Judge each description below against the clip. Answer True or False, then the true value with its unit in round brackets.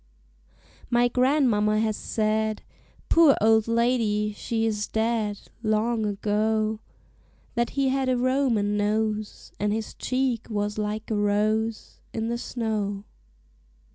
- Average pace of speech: False (120 wpm)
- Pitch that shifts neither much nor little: False (2.0 semitones)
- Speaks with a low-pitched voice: False (220 Hz)